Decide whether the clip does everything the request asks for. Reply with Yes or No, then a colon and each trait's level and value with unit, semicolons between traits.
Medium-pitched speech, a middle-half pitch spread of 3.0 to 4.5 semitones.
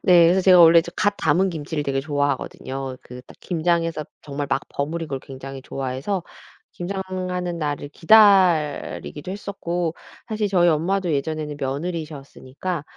Yes: medium, 165 Hz; average, 4.1 semitones